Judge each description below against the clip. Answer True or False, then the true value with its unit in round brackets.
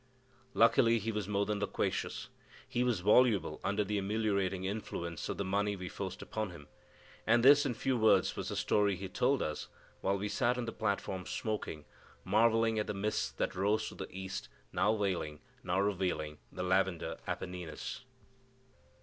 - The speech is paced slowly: False (170 wpm)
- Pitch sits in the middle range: False (100 Hz)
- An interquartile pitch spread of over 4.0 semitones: False (2.9 semitones)